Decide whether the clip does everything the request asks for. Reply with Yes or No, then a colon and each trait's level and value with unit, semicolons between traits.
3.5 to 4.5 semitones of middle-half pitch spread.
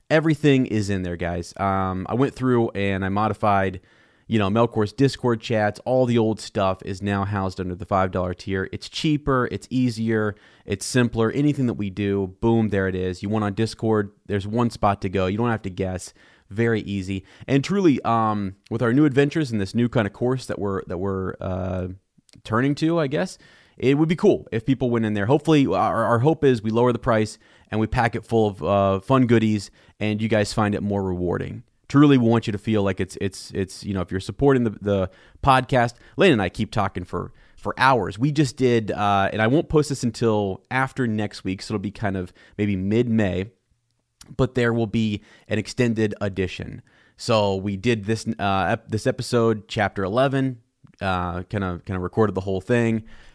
Yes: average, 3.8 semitones